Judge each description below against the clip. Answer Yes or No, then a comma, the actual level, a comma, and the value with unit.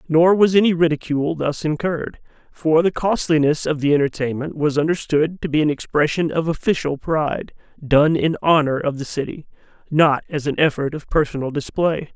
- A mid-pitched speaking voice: Yes, medium, 155 Hz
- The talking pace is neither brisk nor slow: Yes, average, 170 wpm